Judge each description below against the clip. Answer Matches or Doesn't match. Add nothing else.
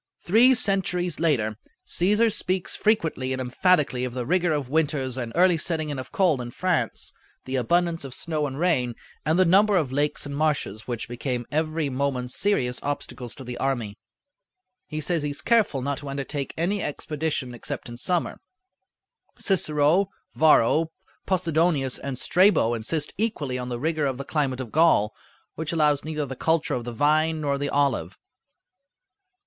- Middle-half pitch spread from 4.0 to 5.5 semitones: Matches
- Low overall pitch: Doesn't match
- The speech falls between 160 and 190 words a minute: Matches